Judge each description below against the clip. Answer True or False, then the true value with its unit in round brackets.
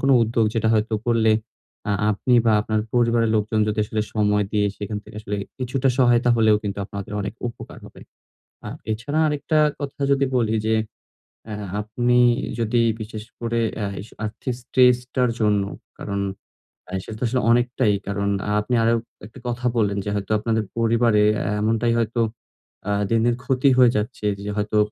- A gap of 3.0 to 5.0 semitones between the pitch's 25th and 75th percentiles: False (2.5 semitones)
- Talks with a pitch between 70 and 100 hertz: False (115 Hz)